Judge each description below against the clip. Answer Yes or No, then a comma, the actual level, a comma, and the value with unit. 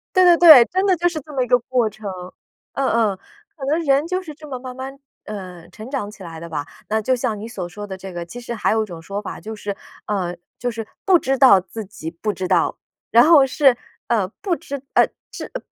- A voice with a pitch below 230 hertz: No, high, 235 Hz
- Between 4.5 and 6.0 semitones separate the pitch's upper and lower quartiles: Yes, wide, 5.6 semitones